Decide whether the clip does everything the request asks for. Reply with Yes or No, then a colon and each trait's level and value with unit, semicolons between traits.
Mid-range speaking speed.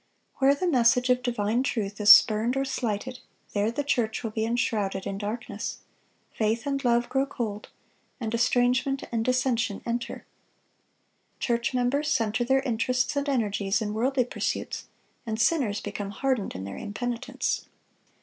Yes: average, 150 wpm